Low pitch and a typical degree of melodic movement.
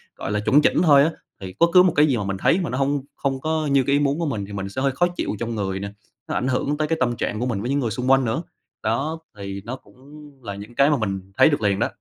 No: low, 130 Hz; wide, 5.9 semitones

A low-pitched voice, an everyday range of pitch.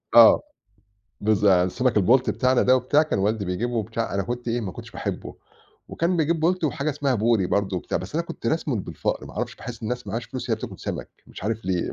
Yes: low, 120 Hz; average, 4.2 semitones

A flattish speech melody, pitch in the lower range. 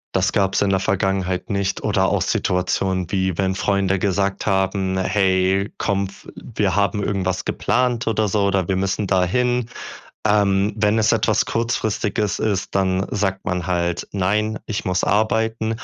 Yes: narrow, 2.0 semitones; low, 100 Hz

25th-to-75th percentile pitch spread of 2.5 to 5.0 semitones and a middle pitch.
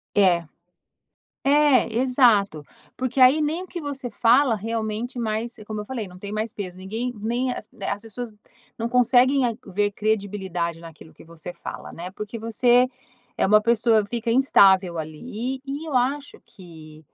No: average, 4.3 semitones; high, 225 Hz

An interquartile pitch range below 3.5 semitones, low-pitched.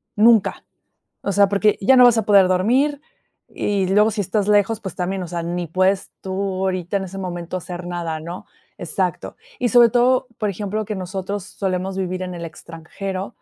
No: average, 2.7 semitones; high, 195 Hz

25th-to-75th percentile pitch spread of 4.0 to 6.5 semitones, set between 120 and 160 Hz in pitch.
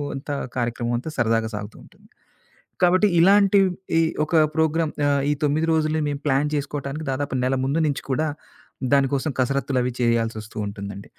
Yes: average, 4.6 semitones; medium, 140 Hz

